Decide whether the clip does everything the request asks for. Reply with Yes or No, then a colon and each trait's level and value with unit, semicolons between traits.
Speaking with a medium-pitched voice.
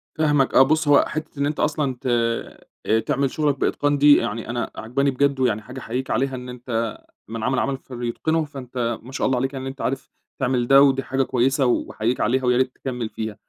No: low, 130 Hz